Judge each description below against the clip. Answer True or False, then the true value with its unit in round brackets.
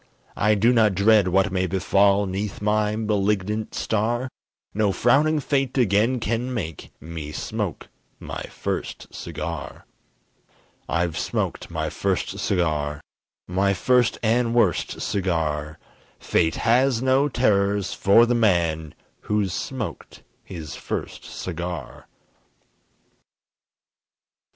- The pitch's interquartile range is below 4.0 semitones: False (4.5 semitones)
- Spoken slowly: True (110 wpm)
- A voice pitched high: False (100 Hz)